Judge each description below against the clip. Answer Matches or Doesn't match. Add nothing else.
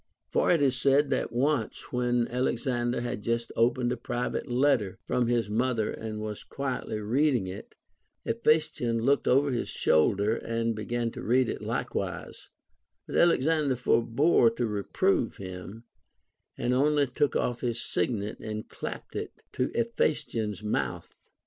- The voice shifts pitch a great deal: Doesn't match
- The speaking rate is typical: Matches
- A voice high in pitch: Doesn't match